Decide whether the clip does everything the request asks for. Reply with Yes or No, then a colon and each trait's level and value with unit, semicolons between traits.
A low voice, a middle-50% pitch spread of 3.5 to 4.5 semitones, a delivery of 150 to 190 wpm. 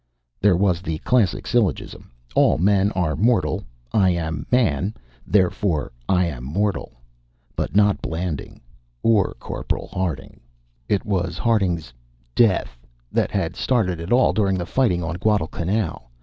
No: very low, 95 Hz; average, 3.9 semitones; slow, 135 wpm